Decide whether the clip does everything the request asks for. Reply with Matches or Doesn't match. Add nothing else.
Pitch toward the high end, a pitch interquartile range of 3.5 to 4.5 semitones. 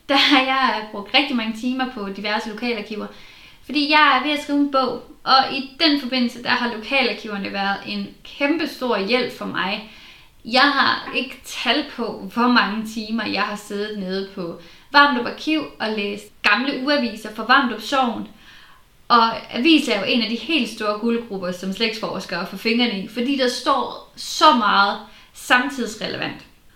Matches